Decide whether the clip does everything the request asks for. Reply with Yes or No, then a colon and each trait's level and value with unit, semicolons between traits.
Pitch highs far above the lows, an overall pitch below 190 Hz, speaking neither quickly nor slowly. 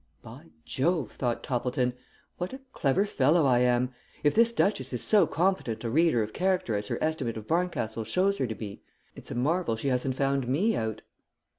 Yes: wide, 6.7 semitones; low, 135 Hz; average, 190 wpm